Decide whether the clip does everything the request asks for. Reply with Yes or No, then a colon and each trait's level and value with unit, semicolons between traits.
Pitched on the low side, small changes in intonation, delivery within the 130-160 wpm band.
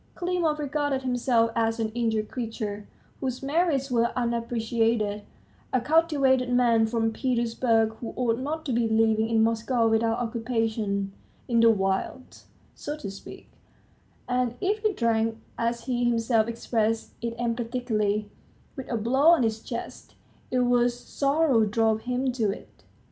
No: high, 235 Hz; narrow, 2.3 semitones; average, 145 wpm